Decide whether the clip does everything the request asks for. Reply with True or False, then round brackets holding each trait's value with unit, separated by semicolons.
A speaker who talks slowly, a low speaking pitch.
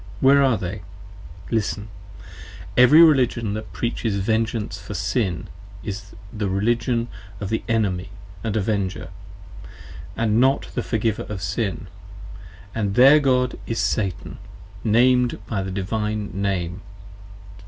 True (120 wpm; 110 Hz)